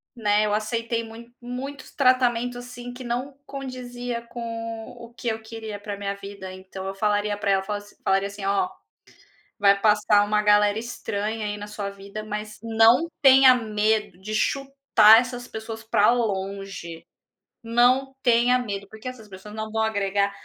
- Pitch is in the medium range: No, high, 220 Hz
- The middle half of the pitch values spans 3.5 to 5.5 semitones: No, average, 2.9 semitones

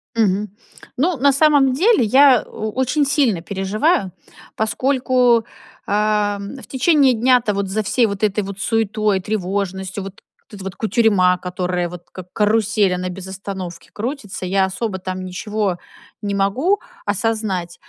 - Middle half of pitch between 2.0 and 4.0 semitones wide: No, average, 4.4 semitones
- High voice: Yes, high, 210 Hz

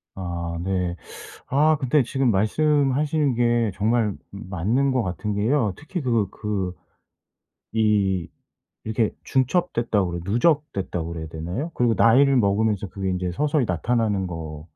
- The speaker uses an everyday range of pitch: No, wide, 5.9 semitones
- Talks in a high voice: No, low, 110 Hz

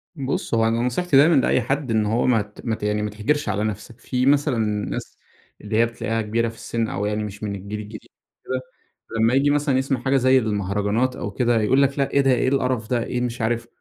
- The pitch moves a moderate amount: Yes, average, 3.7 semitones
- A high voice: No, low, 115 Hz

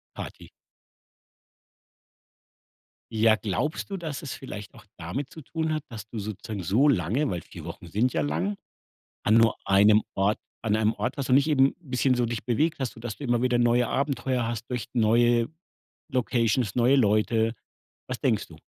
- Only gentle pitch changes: No, average, 3.7 semitones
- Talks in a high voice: No, low, 120 Hz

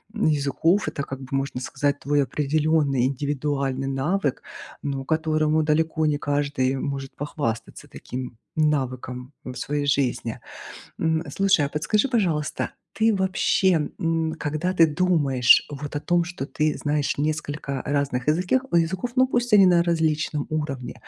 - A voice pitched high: No, medium, 150 Hz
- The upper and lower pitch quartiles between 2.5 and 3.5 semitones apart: Yes, average, 2.9 semitones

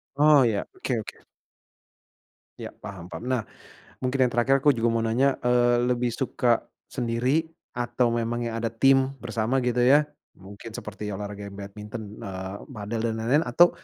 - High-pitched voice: No, low, 120 Hz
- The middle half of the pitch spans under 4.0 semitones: Yes, average, 2.9 semitones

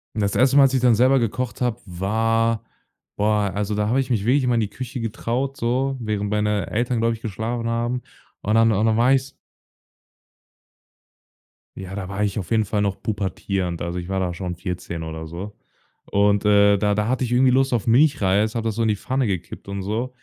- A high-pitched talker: No, low, 110 Hz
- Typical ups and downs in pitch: Yes, average, 3.4 semitones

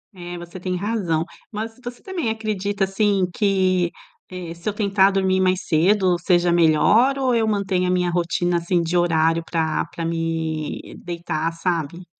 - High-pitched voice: No, medium, 180 Hz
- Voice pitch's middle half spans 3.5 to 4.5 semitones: No, average, 3.0 semitones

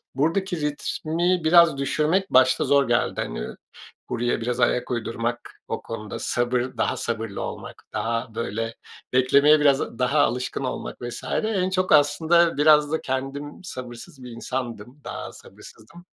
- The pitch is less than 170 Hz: Yes, low, 135 Hz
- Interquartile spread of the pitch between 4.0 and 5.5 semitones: Yes, average, 4.5 semitones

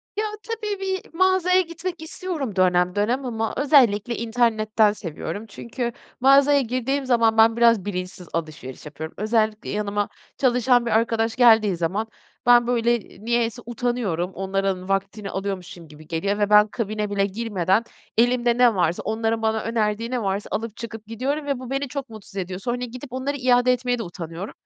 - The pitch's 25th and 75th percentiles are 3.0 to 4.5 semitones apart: Yes, average, 3.7 semitones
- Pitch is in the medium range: No, high, 225 Hz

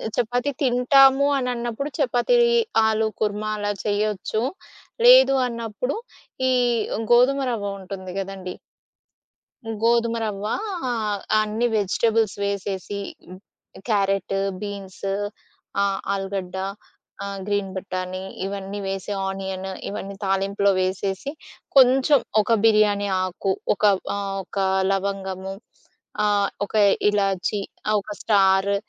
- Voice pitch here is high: Yes, high, 205 Hz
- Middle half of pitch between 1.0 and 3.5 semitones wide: Yes, average, 2.8 semitones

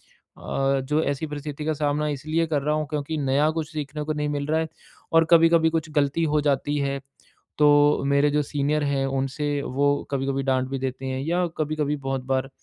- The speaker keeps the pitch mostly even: Yes, narrow, 2.0 semitones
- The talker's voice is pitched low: No, medium, 145 Hz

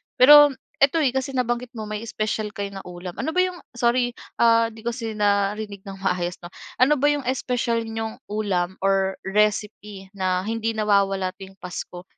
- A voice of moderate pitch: No, high, 215 Hz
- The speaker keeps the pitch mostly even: No, average, 3.8 semitones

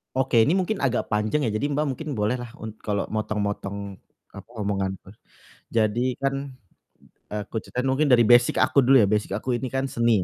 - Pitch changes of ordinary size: Yes, average, 4.2 semitones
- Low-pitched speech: Yes, low, 115 Hz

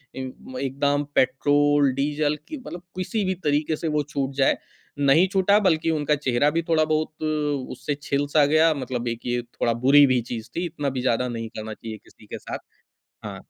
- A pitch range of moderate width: Yes, average, 3.2 semitones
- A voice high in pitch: No, medium, 145 Hz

